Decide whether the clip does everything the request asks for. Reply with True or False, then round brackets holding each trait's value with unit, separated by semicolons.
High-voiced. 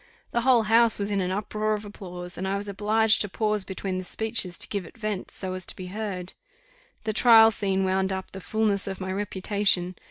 True (200 Hz)